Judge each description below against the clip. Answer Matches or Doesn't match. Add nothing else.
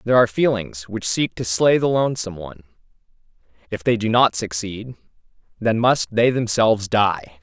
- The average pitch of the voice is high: Doesn't match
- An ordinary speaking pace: Matches